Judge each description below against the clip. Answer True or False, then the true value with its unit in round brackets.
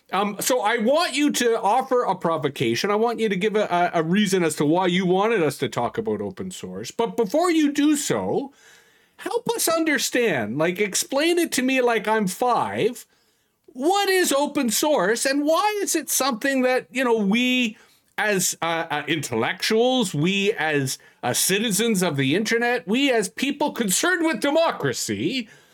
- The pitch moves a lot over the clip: True (6.6 semitones)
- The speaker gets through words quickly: False (175 wpm)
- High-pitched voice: True (230 Hz)